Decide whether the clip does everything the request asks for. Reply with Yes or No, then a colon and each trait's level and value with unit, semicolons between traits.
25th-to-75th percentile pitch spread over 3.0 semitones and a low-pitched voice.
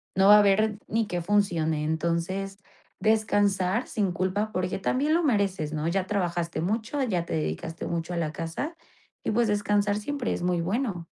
No: average, 3.8 semitones; high, 195 Hz